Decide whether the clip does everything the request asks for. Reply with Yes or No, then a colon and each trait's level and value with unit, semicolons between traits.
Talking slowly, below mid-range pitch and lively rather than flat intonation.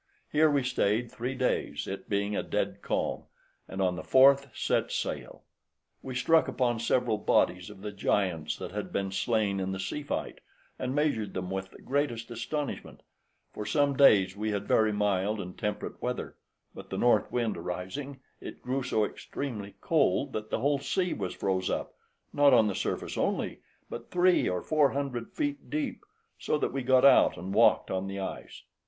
No: average, 185 wpm; low, 115 Hz; wide, 5.9 semitones